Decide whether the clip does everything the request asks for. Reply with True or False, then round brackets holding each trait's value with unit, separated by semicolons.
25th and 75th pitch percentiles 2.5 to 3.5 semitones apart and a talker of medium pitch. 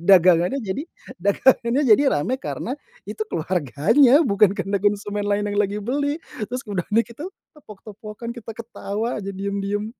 False (3.2 semitones; 210 Hz)